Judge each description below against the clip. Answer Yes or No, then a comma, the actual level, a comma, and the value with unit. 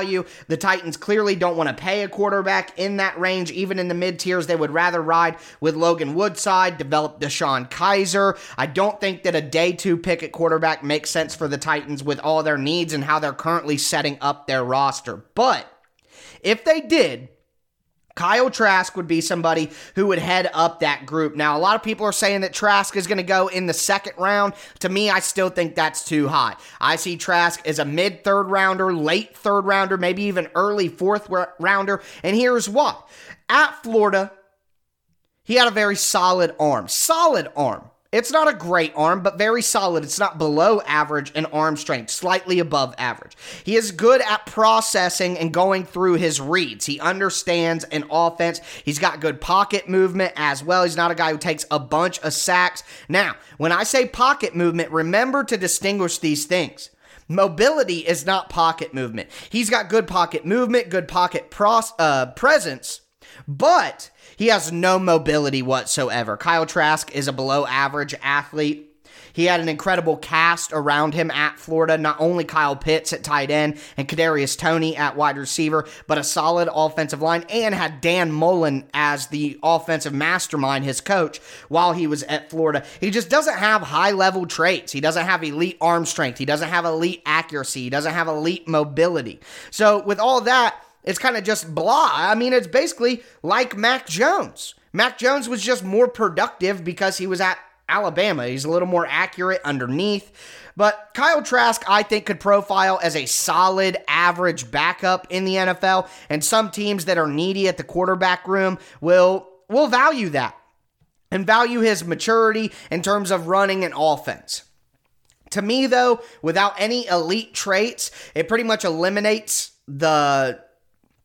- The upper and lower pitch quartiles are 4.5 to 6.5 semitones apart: No, average, 4.0 semitones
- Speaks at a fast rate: No, average, 175 wpm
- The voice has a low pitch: No, medium, 175 Hz